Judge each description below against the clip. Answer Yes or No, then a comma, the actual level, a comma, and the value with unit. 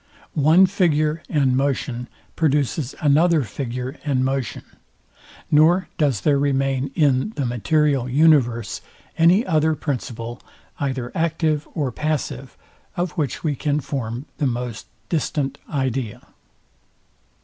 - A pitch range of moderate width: Yes, average, 3.4 semitones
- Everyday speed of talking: No, slow, 115 wpm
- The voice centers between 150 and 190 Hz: No, medium, 140 Hz